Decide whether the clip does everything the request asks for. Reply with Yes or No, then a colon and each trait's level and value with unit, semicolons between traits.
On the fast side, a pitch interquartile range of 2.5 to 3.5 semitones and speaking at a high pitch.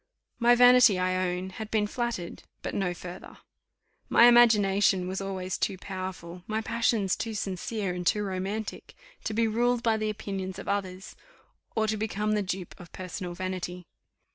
No: average, 165 wpm; average, 3.0 semitones; high, 195 Hz